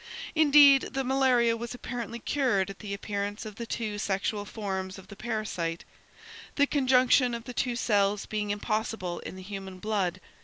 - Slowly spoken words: No, average, 165 wpm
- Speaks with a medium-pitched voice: No, high, 215 Hz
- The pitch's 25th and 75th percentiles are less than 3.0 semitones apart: No, average, 3.7 semitones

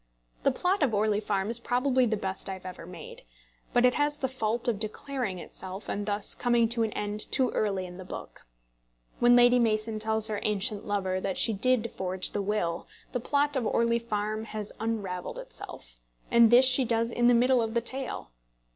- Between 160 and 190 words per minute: No, average, 200 wpm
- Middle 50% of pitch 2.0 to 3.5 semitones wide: Yes, average, 3.1 semitones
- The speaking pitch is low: No, high, 220 Hz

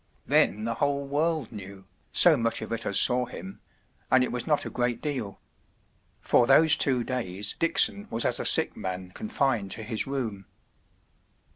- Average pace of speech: Yes, average, 165 wpm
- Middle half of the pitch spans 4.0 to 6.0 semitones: Yes, average, 5.1 semitones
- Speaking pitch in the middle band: No, low, 120 Hz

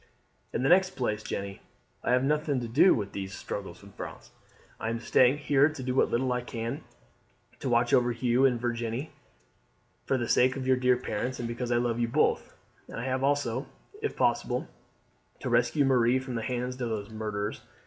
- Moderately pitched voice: No, low, 125 Hz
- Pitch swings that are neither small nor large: No, narrow, 2.2 semitones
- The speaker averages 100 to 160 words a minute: No, average, 200 wpm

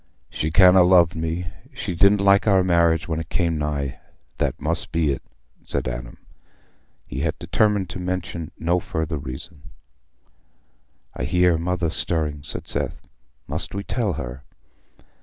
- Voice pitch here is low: Yes, very low, 85 Hz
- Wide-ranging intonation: No, average, 3.2 semitones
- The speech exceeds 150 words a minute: No, average, 145 wpm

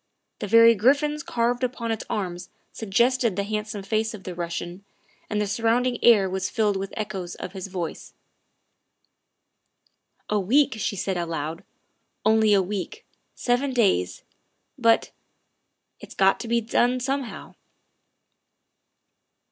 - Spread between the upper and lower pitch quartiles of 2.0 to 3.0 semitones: No, average, 4.0 semitones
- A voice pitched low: No, high, 215 Hz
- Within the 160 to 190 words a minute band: No, slow, 135 wpm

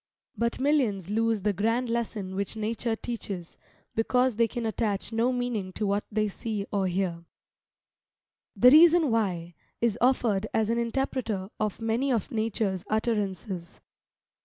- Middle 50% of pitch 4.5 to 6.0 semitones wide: No, average, 3.0 semitones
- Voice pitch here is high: Yes, high, 220 Hz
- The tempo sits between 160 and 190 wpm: No, average, 140 wpm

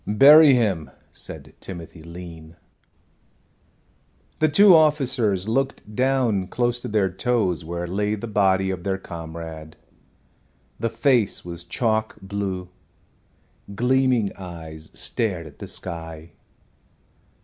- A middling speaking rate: No, slow, 110 wpm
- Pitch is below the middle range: Yes, low, 100 Hz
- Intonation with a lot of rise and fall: Yes, wide, 5.8 semitones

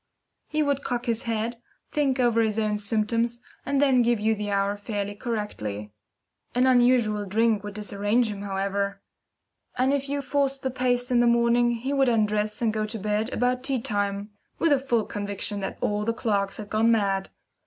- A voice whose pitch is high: Yes, high, 225 Hz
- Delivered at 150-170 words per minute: No, average, 185 wpm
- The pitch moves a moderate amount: Yes, average, 3.1 semitones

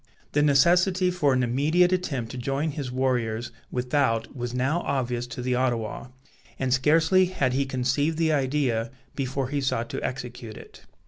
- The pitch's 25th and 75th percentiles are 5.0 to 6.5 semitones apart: No, average, 3.3 semitones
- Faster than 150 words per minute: Yes, average, 160 wpm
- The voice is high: No, low, 130 Hz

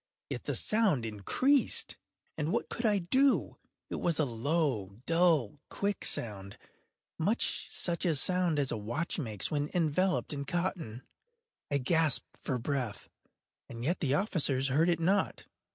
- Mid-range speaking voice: Yes, medium, 155 Hz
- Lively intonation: Yes, wide, 6.0 semitones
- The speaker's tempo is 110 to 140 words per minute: Yes, slow, 135 wpm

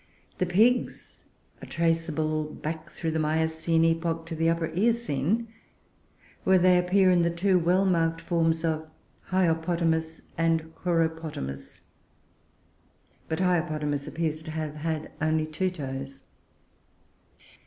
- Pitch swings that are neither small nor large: No, narrow, 1.8 semitones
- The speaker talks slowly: Yes, slow, 120 wpm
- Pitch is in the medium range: Yes, medium, 165 Hz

